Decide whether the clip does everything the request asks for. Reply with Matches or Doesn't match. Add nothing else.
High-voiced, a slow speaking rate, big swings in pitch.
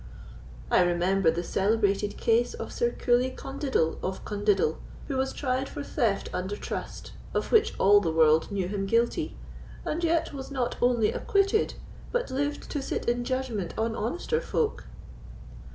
Doesn't match